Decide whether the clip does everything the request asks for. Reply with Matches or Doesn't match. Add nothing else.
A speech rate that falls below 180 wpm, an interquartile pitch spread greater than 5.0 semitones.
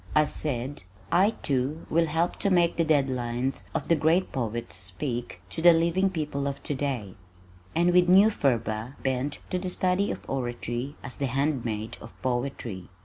Matches